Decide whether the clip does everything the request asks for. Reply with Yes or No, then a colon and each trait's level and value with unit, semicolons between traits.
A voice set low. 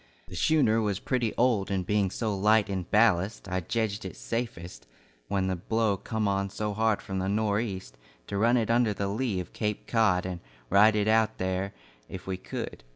Yes: low, 100 Hz